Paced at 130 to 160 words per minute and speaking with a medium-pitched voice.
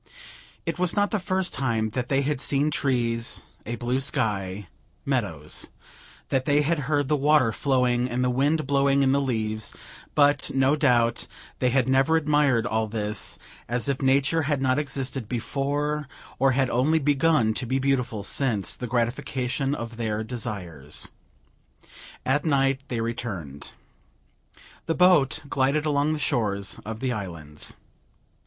No: average, 150 wpm; low, 130 Hz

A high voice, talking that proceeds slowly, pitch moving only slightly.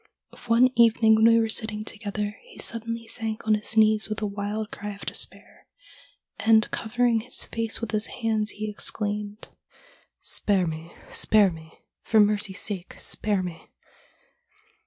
No: high, 215 Hz; average, 155 wpm; narrow, 1.6 semitones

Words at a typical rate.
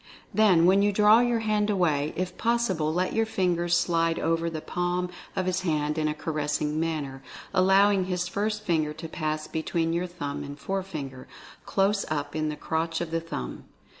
Yes: average, 180 wpm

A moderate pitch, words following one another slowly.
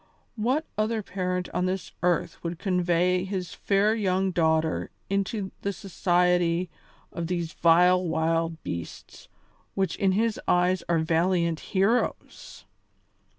Yes: medium, 180 Hz; slow, 120 wpm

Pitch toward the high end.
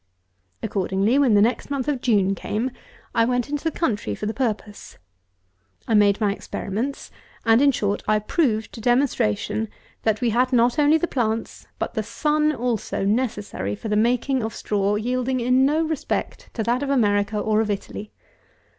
Yes: high, 230 Hz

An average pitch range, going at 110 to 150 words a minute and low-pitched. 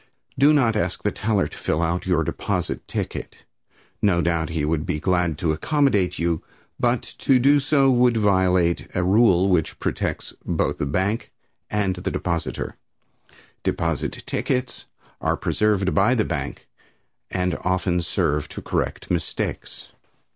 Yes: average, 4.5 semitones; average, 145 wpm; very low, 90 Hz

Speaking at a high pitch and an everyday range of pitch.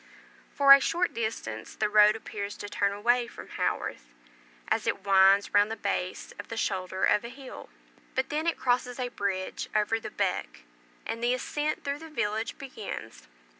Yes: high, 220 Hz; average, 3.9 semitones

